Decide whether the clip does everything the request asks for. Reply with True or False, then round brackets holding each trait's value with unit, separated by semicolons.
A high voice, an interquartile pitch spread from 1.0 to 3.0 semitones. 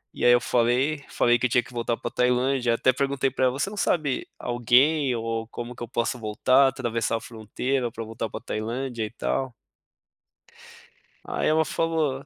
False (125 Hz; 2.5 semitones)